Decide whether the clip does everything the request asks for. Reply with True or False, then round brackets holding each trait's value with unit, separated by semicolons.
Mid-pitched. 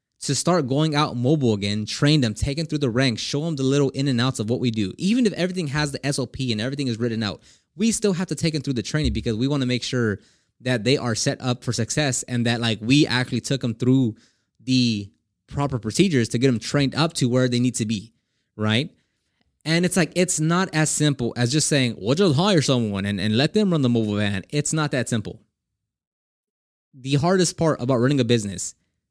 False (130 Hz)